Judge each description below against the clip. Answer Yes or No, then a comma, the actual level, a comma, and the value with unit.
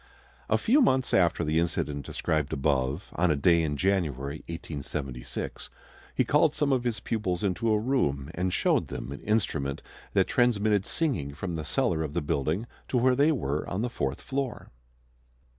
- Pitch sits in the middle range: No, very low, 85 Hz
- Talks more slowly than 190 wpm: Yes, average, 175 wpm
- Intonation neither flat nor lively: No, wide, 8.3 semitones